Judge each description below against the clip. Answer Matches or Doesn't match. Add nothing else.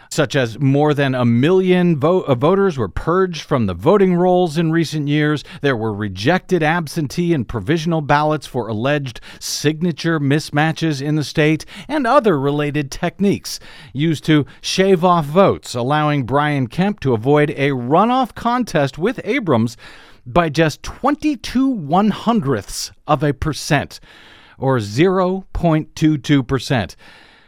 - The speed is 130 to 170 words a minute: Matches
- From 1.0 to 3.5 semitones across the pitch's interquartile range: Doesn't match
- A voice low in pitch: Doesn't match